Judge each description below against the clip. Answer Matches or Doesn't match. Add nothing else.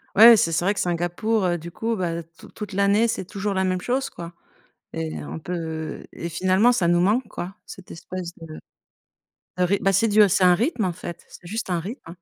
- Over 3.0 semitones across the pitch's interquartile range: Matches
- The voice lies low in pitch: Doesn't match